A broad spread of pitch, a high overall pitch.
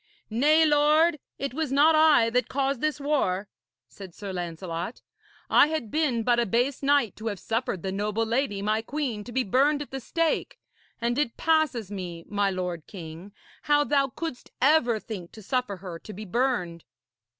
Yes: wide, 6.3 semitones; high, 235 Hz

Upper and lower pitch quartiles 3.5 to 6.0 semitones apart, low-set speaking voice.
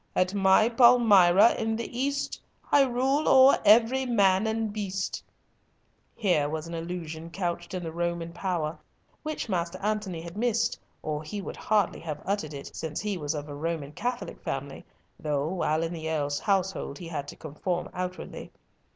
No: average, 5.1 semitones; medium, 180 Hz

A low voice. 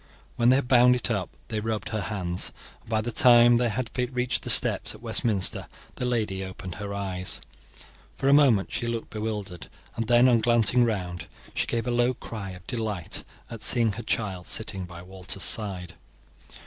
Yes: low, 110 Hz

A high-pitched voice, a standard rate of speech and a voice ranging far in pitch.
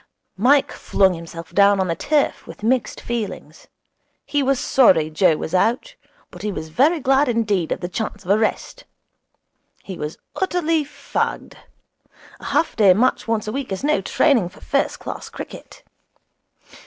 Yes: high, 215 Hz; average, 165 wpm; wide, 6.9 semitones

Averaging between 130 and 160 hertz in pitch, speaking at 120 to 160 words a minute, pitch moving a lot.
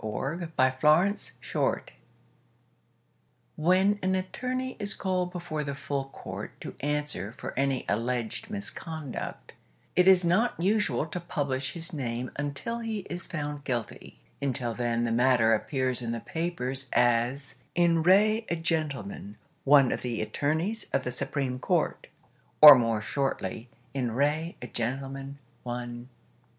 Yes: medium, 140 Hz; average, 140 wpm; wide, 5.9 semitones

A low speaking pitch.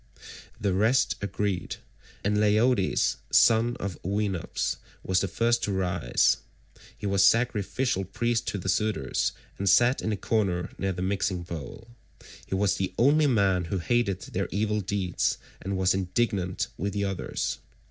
Yes: low, 100 Hz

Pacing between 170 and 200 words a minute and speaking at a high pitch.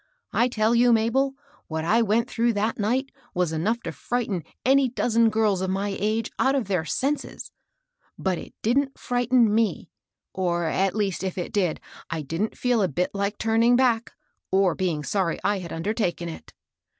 Yes: average, 175 wpm; high, 215 Hz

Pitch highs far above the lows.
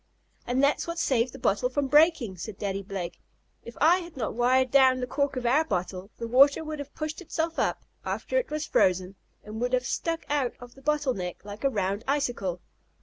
Yes: wide, 5.8 semitones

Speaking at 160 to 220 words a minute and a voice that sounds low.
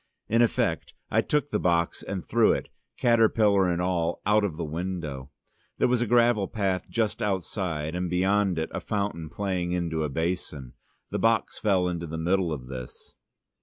Yes: average, 180 wpm; very low, 90 Hz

